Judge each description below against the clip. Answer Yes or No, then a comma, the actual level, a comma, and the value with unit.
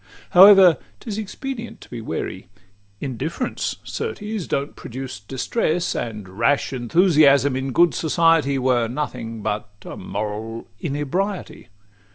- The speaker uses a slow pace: Yes, slow, 120 wpm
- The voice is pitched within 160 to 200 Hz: No, medium, 140 Hz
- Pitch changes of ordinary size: No, wide, 7.0 semitones